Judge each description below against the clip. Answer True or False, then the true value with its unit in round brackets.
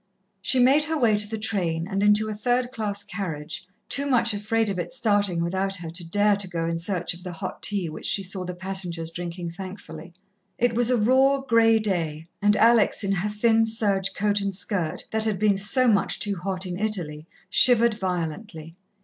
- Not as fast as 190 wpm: False (200 wpm)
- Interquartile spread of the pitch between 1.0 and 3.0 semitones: False (3.8 semitones)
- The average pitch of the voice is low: False (200 Hz)